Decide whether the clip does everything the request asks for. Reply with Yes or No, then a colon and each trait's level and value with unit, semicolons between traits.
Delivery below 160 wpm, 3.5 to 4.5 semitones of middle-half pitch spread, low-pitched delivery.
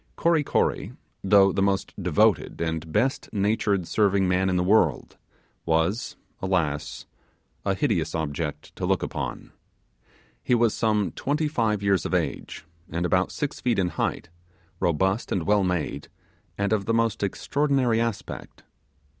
Yes: average, 145 wpm; average, 4.2 semitones; low, 100 Hz